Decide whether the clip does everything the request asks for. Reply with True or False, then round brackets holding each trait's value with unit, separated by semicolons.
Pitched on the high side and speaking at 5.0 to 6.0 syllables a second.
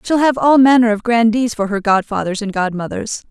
True (225 Hz; 5.4 syllables/s)